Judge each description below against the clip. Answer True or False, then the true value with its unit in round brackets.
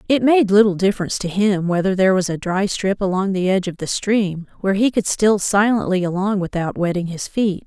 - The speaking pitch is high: True (195 Hz)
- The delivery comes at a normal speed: False (220 wpm)